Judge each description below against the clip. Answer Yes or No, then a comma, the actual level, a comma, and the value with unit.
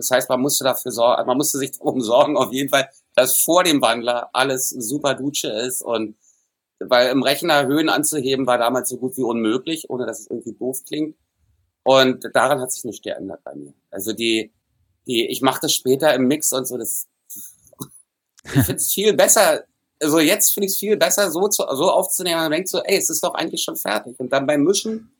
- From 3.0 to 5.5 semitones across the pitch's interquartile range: Yes, average, 3.6 semitones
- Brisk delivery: Yes, fast, 215 wpm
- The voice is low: Yes, low, 130 Hz